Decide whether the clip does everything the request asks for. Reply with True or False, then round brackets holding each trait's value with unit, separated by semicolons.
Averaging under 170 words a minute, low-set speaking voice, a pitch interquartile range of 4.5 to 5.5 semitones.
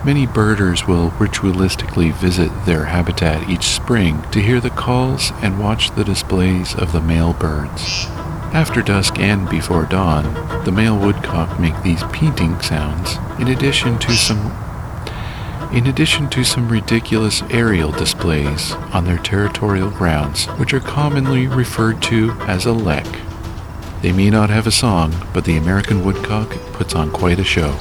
True (155 wpm; 100 Hz; 4.9 semitones)